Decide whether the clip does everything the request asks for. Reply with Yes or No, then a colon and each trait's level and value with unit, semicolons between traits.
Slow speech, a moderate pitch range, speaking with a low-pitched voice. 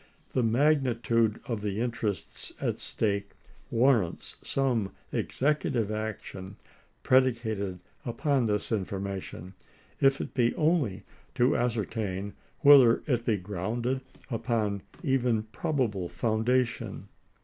Yes: slow, 105 wpm; average, 3.8 semitones; low, 115 Hz